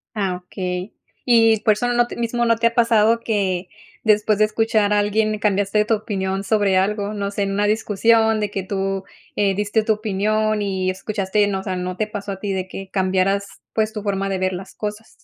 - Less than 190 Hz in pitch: No, high, 205 Hz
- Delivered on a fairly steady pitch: Yes, narrow, 1.9 semitones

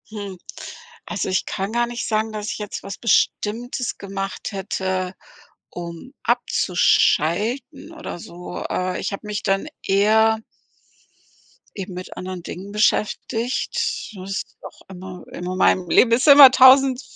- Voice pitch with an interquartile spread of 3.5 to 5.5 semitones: Yes, average, 4.1 semitones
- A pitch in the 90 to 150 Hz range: No, high, 205 Hz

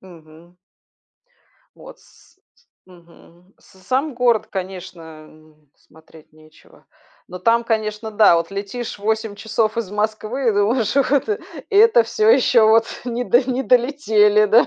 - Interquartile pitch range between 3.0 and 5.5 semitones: Yes, average, 5.0 semitones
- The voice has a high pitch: Yes, high, 215 Hz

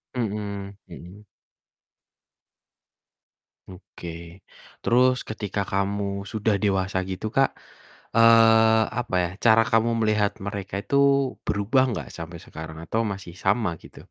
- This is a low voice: Yes, low, 105 Hz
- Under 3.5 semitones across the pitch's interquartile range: Yes, narrow, 2.5 semitones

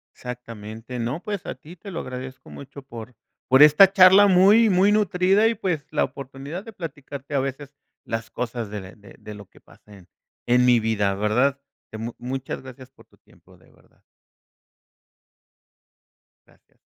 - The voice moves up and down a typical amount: No, wide, 7.4 semitones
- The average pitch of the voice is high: No, low, 135 Hz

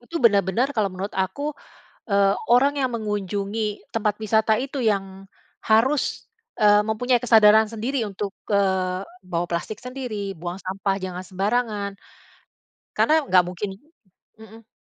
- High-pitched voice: Yes, high, 210 Hz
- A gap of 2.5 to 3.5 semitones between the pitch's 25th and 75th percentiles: Yes, average, 3.2 semitones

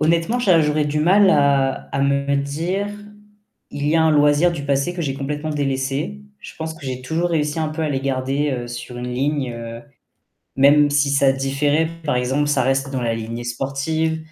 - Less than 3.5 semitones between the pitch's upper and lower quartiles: Yes, average, 2.7 semitones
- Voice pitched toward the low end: No, medium, 145 Hz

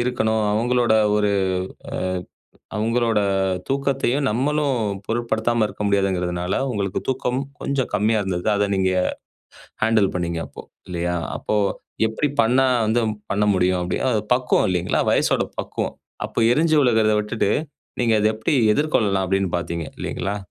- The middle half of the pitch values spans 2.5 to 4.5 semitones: Yes, average, 4.2 semitones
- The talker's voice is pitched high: No, low, 110 Hz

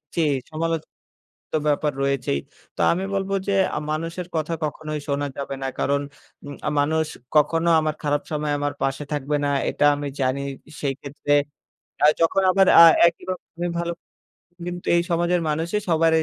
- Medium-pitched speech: Yes, medium, 155 Hz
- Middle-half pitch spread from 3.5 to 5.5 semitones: No, average, 2.8 semitones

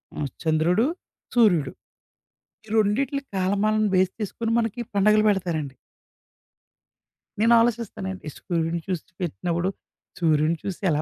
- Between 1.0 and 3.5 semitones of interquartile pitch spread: No, average, 4.2 semitones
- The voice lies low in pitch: No, high, 190 Hz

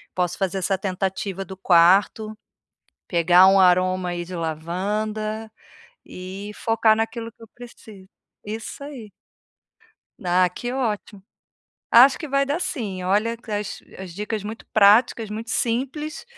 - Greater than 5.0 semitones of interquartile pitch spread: No, average, 3.5 semitones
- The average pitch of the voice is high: Yes, high, 205 Hz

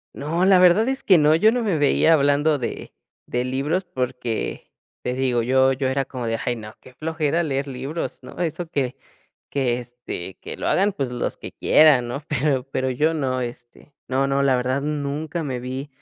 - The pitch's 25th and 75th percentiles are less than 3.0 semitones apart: No, average, 3.8 semitones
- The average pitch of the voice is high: No, medium, 140 Hz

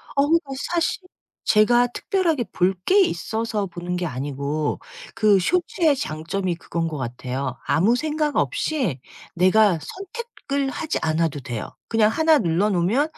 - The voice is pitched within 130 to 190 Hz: No, high, 205 Hz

